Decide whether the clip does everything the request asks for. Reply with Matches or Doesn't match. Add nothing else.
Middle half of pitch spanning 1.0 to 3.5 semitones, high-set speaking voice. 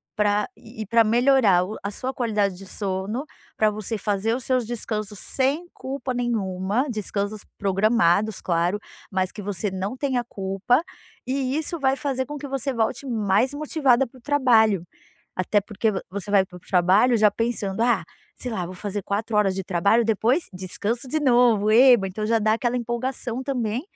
Doesn't match